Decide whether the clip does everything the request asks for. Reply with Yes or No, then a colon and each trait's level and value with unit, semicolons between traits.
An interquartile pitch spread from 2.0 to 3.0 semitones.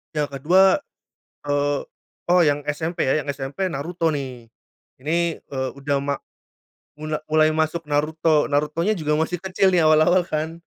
Yes: narrow, 2.6 semitones